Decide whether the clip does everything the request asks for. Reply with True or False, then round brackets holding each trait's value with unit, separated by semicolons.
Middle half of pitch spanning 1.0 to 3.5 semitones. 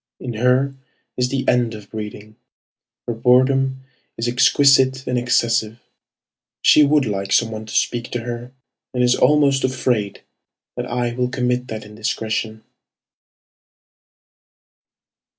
True (2.6 semitones)